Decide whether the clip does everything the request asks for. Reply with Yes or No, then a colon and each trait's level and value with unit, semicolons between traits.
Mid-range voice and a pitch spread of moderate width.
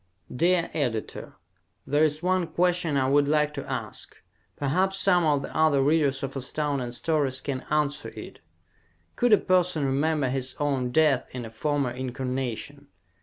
Yes: medium, 145 Hz; average, 3.0 semitones